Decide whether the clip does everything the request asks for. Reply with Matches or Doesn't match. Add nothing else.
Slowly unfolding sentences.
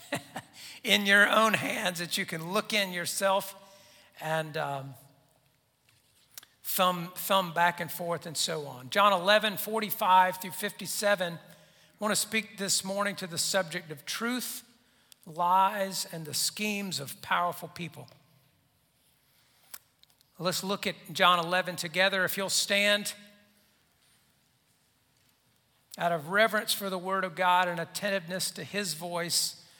Matches